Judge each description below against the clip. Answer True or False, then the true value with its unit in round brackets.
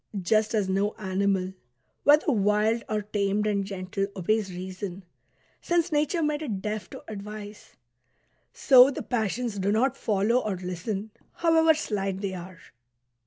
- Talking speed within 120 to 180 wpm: True (140 wpm)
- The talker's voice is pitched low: False (210 Hz)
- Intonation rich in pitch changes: False (3.4 semitones)